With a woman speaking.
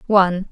Yes: female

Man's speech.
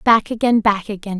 No: female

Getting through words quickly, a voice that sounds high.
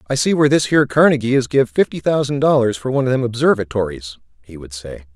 No: fast, 220 wpm; low, 120 Hz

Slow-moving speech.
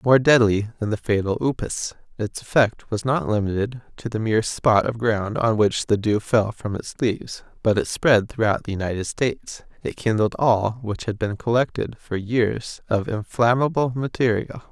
No: average, 180 wpm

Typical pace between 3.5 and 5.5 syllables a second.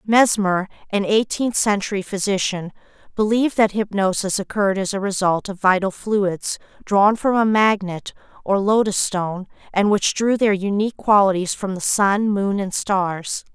Yes: 4.6 syllables/s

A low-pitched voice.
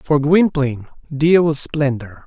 No: medium, 145 Hz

